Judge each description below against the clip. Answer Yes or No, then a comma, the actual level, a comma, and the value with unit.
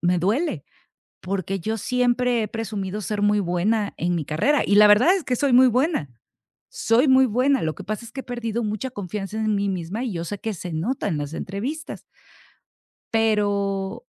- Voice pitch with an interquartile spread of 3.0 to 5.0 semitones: Yes, average, 4.2 semitones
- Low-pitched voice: No, high, 210 Hz